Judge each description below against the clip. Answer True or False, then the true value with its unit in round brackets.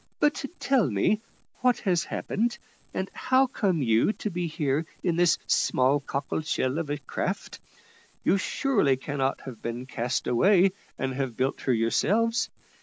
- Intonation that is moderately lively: False (7.5 semitones)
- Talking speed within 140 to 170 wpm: True (155 wpm)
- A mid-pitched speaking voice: True (155 Hz)